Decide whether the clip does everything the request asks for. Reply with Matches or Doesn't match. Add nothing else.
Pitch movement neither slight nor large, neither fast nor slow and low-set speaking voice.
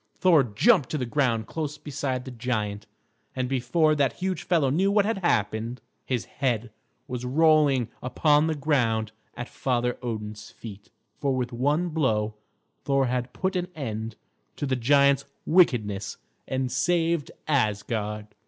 Matches